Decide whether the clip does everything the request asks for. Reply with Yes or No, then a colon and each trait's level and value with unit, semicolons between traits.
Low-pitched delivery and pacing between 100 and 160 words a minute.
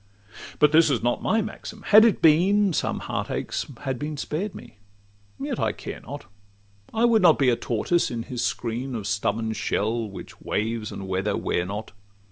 No: low, 125 Hz; average, 185 wpm